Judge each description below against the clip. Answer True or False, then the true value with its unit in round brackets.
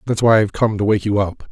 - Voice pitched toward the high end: False (105 Hz)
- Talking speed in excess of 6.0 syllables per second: True (6.9 syllables/s)